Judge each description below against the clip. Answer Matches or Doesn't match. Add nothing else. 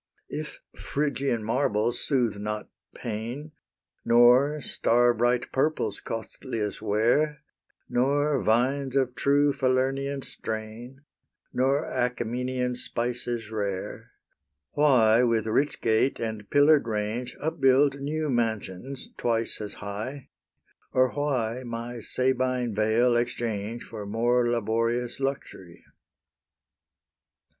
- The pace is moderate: Doesn't match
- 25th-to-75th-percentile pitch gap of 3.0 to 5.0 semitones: Matches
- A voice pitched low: Matches